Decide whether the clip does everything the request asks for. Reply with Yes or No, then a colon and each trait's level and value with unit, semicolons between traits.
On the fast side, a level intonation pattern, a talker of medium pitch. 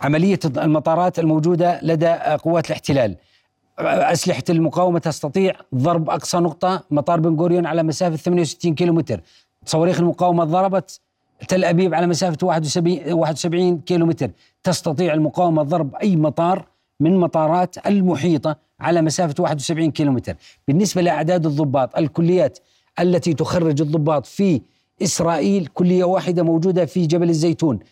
No: average, 120 wpm; narrow, 2.3 semitones; medium, 170 Hz